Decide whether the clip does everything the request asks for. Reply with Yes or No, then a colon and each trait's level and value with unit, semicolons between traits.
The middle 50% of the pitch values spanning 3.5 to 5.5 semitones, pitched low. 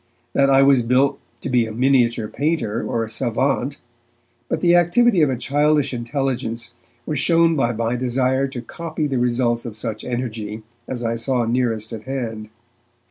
No: average, 3.0 semitones; low, 125 Hz